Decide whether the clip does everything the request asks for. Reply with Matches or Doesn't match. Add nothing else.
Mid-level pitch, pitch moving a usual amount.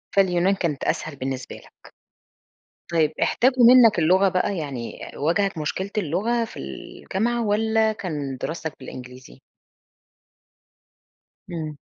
Doesn't match